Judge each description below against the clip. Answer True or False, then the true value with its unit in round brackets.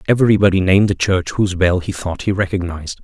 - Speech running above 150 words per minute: True (200 wpm)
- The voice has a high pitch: False (95 Hz)